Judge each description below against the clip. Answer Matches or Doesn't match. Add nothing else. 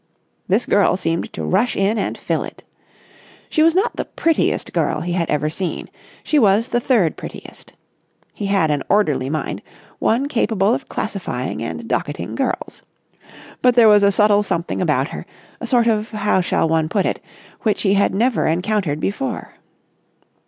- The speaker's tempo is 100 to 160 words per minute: Doesn't match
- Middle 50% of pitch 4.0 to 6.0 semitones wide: Matches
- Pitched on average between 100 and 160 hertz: Doesn't match